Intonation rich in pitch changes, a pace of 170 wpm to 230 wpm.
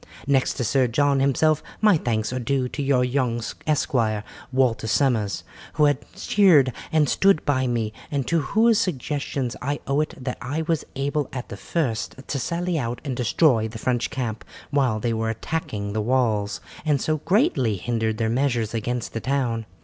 No: average, 4.1 semitones; average, 180 wpm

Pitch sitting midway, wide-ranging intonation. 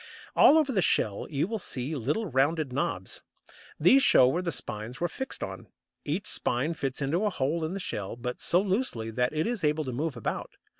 Yes: medium, 150 Hz; wide, 6.5 semitones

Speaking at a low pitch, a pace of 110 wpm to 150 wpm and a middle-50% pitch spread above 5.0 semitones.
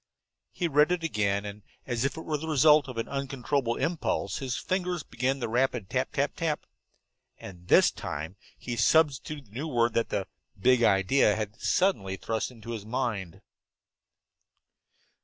No: low, 125 Hz; average, 160 wpm; wide, 5.6 semitones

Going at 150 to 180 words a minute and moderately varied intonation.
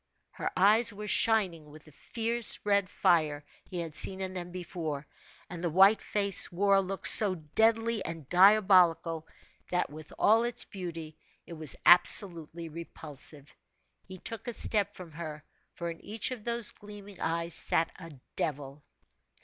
Yes: average, 155 wpm; average, 4.1 semitones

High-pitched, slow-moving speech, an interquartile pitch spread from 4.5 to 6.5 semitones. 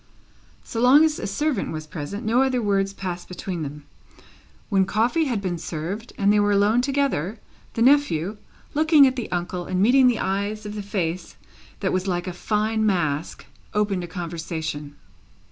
No: high, 200 Hz; average, 175 wpm; average, 4.8 semitones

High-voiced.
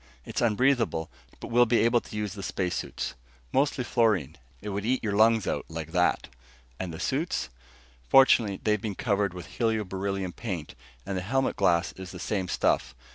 No: low, 105 Hz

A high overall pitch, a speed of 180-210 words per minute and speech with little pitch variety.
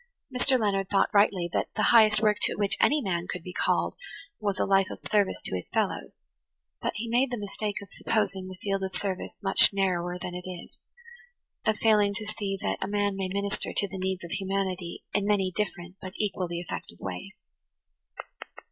Yes: high, 195 Hz; average, 190 wpm; narrow, 2.2 semitones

